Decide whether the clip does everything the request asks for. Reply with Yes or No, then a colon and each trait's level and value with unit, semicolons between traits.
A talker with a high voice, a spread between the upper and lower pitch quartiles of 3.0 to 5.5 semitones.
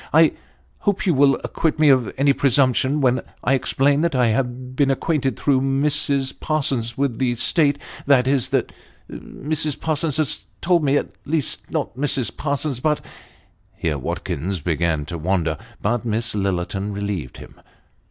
No: low, 130 Hz; average, 4.4 semitones